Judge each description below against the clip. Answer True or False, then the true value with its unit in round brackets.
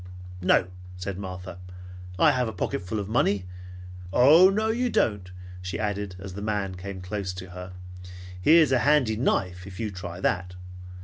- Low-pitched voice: True (100 Hz)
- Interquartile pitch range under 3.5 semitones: False (4.5 semitones)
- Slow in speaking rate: False (160 wpm)